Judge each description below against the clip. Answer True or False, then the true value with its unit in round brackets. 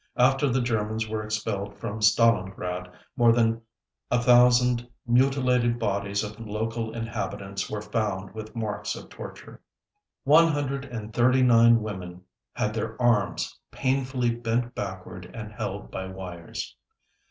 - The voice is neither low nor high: False (115 Hz)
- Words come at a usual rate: False (130 wpm)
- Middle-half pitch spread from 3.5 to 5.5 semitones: False (2.9 semitones)